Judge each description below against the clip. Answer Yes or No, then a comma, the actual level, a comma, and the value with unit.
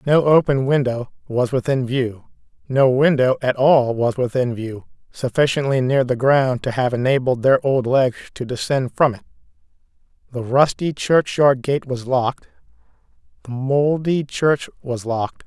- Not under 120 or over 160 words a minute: Yes, average, 145 wpm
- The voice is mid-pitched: No, low, 130 Hz